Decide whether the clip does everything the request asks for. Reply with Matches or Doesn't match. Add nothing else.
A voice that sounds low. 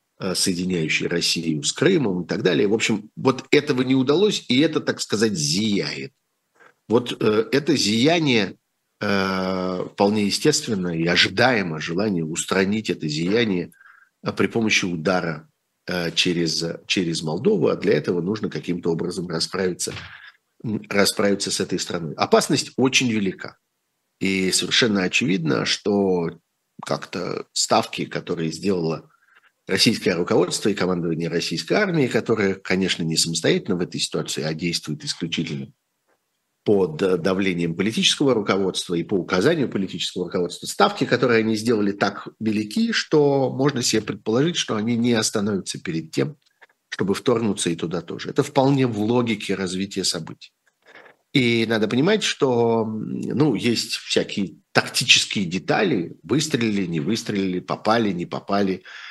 Matches